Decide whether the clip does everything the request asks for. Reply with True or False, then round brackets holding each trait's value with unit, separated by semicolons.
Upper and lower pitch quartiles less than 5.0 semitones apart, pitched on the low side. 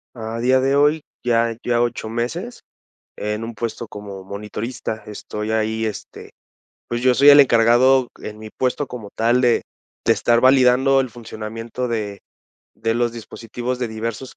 True (2.4 semitones; 115 Hz)